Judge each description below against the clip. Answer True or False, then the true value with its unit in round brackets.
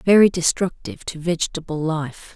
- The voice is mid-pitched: True (170 Hz)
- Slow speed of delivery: True (125 wpm)